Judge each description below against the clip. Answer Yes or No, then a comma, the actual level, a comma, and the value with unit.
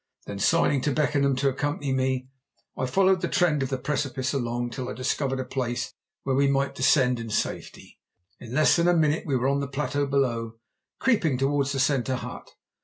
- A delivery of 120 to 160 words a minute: No, average, 195 wpm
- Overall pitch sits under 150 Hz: Yes, low, 135 Hz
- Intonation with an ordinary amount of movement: No, narrow, 2.1 semitones